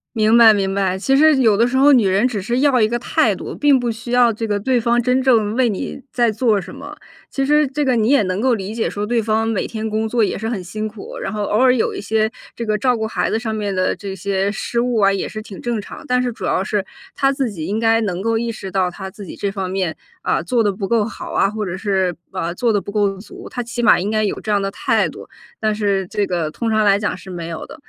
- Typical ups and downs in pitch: Yes, average, 3.3 semitones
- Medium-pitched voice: No, high, 215 Hz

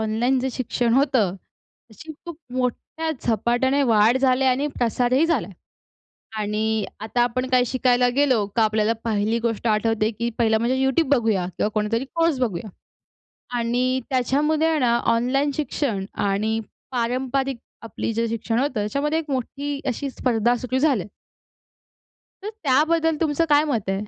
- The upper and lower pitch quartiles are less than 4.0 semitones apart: Yes, average, 3.6 semitones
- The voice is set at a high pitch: Yes, high, 245 Hz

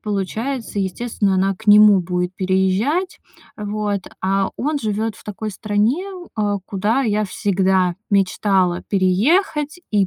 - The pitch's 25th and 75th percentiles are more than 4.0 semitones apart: No, narrow, 2.6 semitones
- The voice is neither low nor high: No, high, 205 Hz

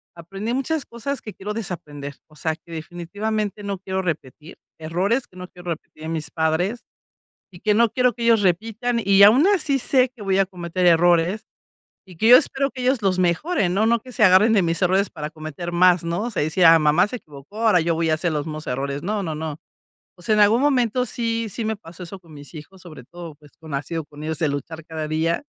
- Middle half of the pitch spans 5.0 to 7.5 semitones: Yes, wide, 5.4 semitones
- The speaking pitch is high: No, medium, 180 Hz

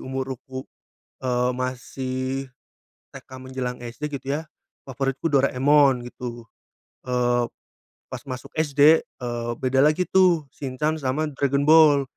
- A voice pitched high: No, low, 130 Hz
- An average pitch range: No, narrow, 2.3 semitones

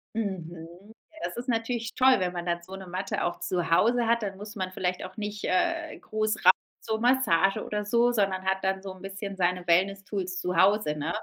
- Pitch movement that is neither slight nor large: Yes, average, 3.2 semitones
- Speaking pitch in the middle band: No, high, 195 Hz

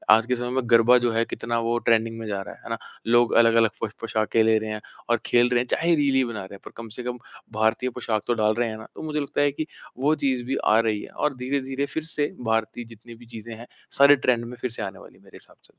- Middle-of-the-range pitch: No, low, 120 Hz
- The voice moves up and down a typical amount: No, narrow, 2.3 semitones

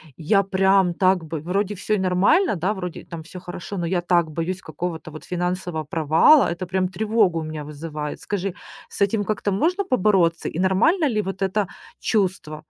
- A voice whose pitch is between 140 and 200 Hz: Yes, medium, 185 Hz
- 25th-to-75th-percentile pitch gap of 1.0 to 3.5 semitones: Yes, average, 3.2 semitones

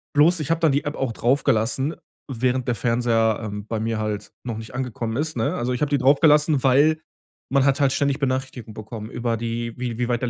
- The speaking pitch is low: Yes, low, 125 Hz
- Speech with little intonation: No, average, 3.6 semitones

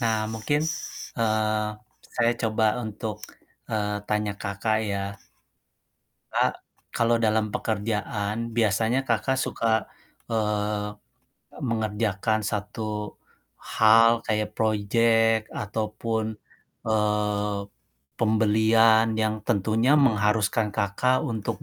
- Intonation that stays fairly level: Yes, narrow, 1.3 semitones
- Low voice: Yes, low, 110 Hz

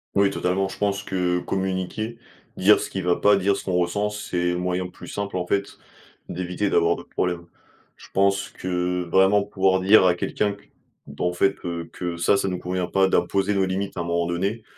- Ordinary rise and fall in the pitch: No, narrow, 1.9 semitones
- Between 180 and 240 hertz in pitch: No, very low, 95 Hz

